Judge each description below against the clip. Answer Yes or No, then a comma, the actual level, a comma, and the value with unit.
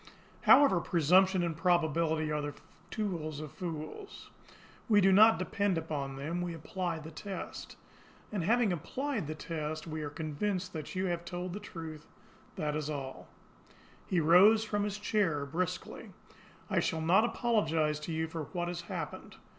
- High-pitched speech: No, medium, 170 Hz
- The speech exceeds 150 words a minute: Yes, average, 160 wpm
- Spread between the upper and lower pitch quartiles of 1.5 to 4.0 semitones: Yes, average, 3.6 semitones